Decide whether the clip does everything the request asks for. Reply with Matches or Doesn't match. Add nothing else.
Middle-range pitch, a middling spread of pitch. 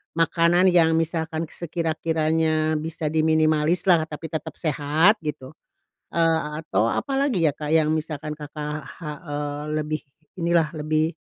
Doesn't match